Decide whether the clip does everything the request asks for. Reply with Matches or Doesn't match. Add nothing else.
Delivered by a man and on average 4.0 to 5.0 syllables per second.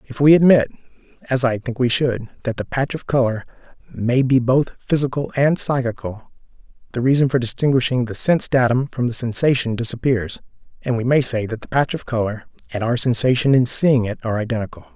Doesn't match